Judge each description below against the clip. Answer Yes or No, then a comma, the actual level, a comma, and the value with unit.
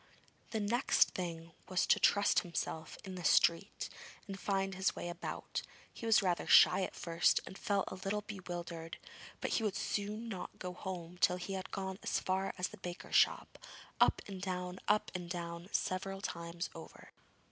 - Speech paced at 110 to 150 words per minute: No, average, 175 wpm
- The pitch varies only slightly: Yes, narrow, 2.1 semitones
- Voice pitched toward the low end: No, medium, 185 Hz